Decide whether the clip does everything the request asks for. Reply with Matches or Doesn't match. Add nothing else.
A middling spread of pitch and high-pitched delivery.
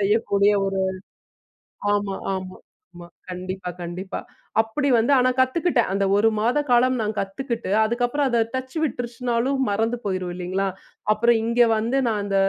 Matches